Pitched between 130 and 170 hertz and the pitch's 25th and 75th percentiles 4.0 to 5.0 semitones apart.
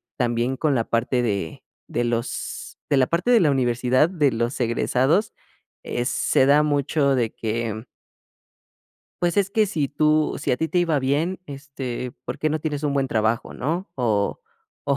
Yes: low, 135 Hz; average, 4.3 semitones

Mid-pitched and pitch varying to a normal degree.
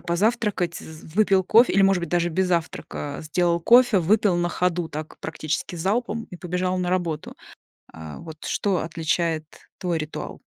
Yes: medium, 175 Hz; average, 3.1 semitones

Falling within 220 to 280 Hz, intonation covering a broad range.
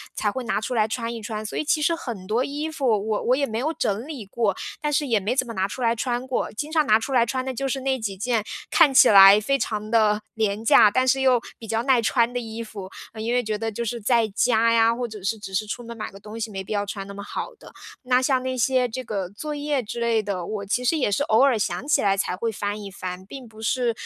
No: high, 230 Hz; average, 3.5 semitones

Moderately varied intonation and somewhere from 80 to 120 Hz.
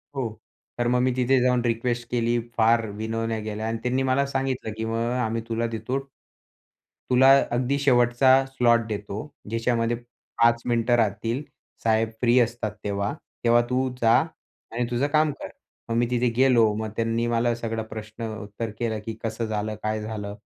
No: narrow, 1.9 semitones; low, 115 Hz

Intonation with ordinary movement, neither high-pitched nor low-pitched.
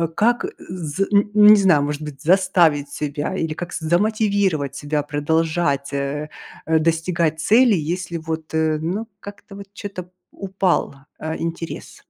Yes: average, 4.2 semitones; medium, 165 Hz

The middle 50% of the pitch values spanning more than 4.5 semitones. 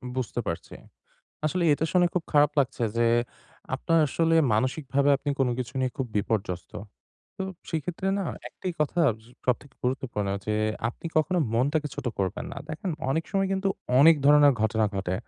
Yes: wide, 5.6 semitones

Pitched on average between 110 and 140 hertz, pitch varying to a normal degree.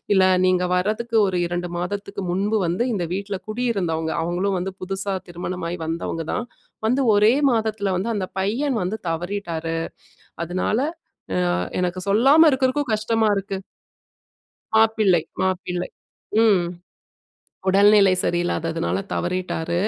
No: high, 190 Hz; average, 3.5 semitones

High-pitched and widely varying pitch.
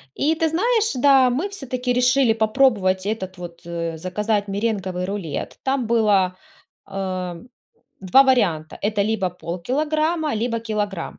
Yes: high, 215 Hz; wide, 5.9 semitones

